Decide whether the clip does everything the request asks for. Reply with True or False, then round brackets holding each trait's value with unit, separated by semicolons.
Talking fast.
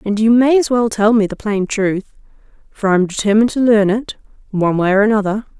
True (225 wpm)